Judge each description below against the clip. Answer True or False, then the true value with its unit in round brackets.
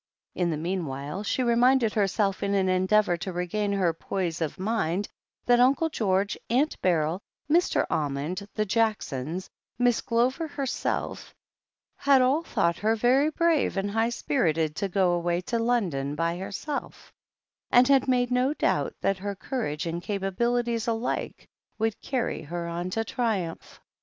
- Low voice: False (205 Hz)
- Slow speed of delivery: False (150 wpm)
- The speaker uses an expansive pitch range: True (5.7 semitones)